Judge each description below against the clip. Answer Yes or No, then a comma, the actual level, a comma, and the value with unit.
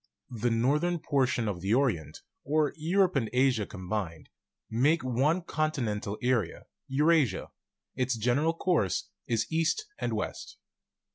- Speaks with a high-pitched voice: No, low, 130 Hz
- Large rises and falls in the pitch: Yes, wide, 5.9 semitones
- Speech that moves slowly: Yes, slow, 130 wpm